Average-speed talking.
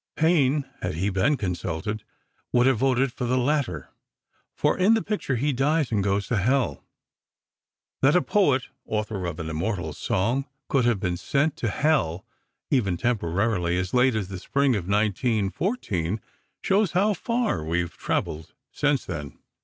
Yes: average, 160 wpm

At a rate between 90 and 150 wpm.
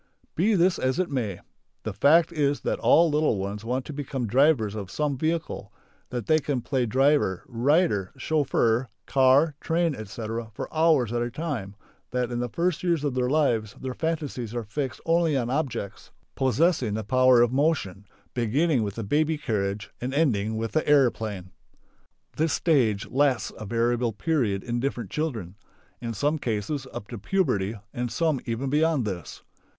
No: average, 170 wpm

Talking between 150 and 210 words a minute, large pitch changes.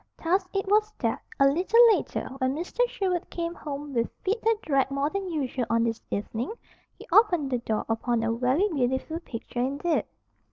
Yes: average, 185 wpm; wide, 6.9 semitones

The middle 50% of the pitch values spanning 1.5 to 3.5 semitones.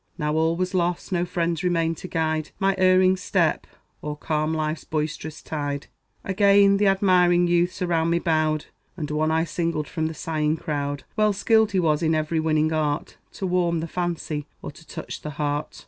Yes: average, 2.7 semitones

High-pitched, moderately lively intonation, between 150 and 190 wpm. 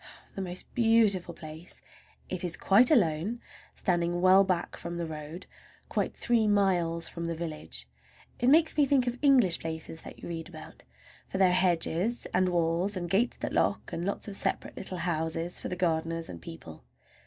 No: medium, 175 Hz; average, 3.3 semitones; average, 180 wpm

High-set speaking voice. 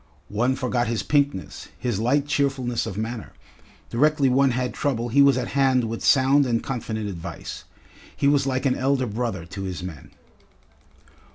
No: low, 125 Hz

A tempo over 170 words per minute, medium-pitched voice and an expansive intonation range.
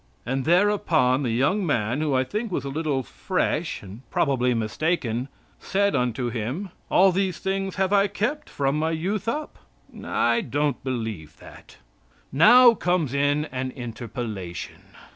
No: average, 145 wpm; medium, 145 Hz; wide, 7.5 semitones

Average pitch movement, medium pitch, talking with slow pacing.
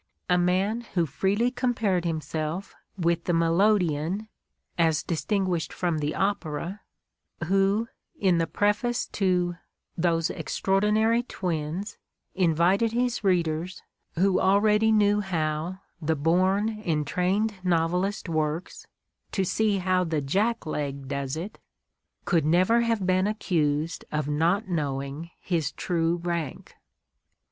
Yes: average, 3.9 semitones; medium, 180 Hz; slow, 120 wpm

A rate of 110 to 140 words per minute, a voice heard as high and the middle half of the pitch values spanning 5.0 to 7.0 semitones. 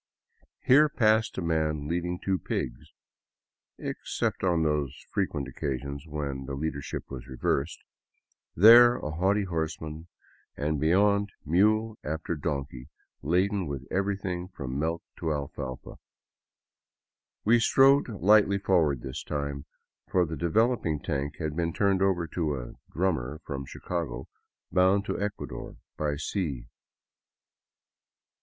No: slow, 135 wpm; very low, 80 Hz; wide, 5.4 semitones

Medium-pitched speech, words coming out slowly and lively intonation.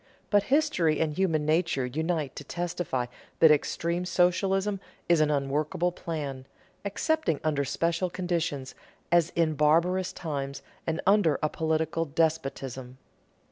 No: medium, 160 Hz; slow, 125 wpm; average, 3.1 semitones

